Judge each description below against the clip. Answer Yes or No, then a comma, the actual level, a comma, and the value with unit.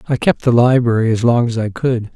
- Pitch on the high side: No, low, 120 Hz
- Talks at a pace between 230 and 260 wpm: Yes, fast, 250 wpm